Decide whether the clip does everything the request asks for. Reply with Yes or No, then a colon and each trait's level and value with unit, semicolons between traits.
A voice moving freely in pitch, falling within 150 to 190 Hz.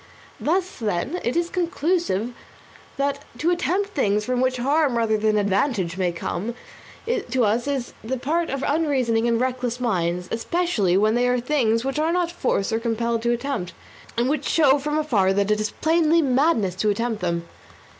No: wide, 5.9 semitones; high, 245 Hz